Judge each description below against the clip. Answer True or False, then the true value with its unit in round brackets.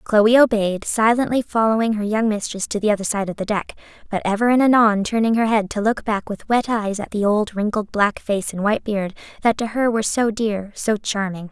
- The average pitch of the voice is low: False (215 Hz)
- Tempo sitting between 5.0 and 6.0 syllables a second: True (5.4 syllables/s)